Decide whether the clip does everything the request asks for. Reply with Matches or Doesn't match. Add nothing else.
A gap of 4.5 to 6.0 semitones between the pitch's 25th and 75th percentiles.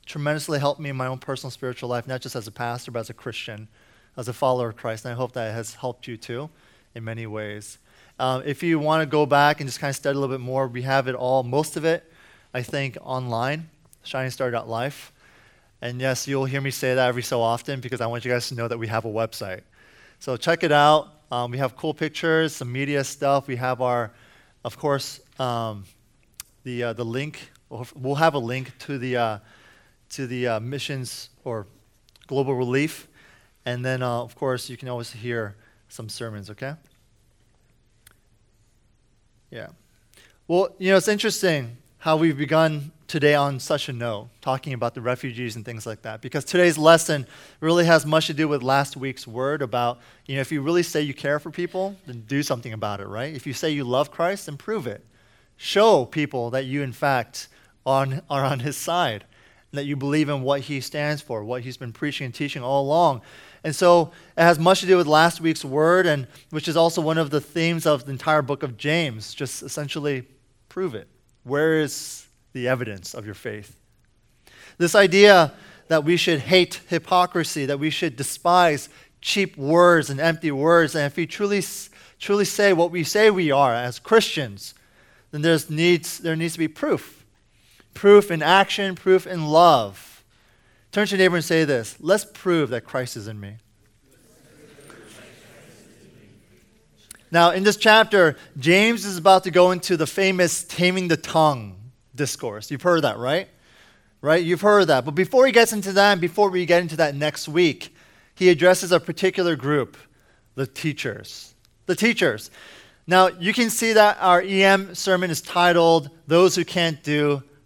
Matches